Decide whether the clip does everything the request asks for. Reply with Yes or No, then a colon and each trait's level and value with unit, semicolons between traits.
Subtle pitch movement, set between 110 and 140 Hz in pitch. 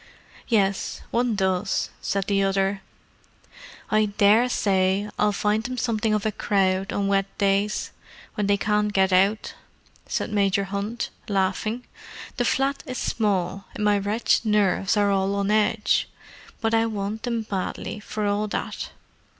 No: narrow, 1.7 semitones; high, 205 Hz